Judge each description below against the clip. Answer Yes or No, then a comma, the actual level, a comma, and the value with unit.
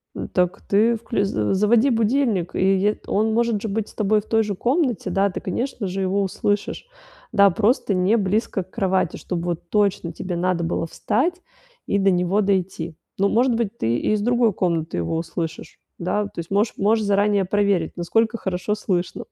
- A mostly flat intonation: No, average, 3.3 semitones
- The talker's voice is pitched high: Yes, high, 200 Hz